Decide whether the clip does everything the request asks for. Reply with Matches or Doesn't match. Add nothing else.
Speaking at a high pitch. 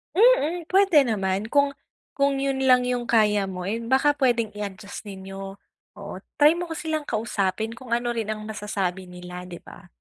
Matches